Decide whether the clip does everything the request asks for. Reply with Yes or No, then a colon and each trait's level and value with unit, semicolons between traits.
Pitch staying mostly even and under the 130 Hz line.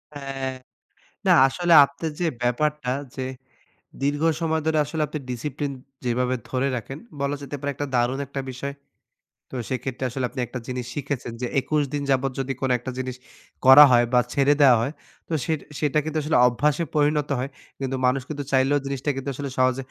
No: narrow, 2.2 semitones; low, 135 Hz